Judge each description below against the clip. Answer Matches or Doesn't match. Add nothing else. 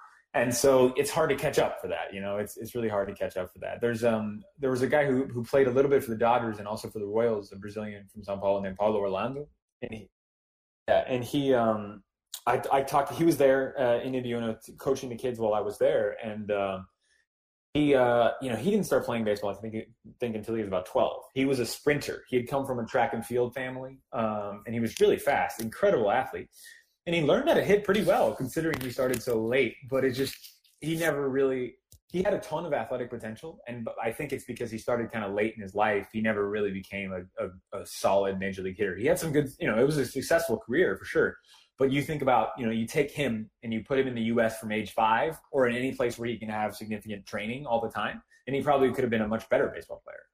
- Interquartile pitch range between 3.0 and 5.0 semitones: Matches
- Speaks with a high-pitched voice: Doesn't match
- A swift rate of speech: Matches